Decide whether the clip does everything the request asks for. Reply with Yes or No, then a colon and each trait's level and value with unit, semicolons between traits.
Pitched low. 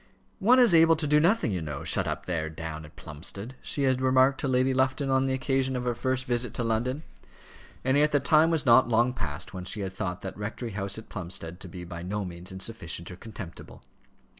Yes: low, 115 Hz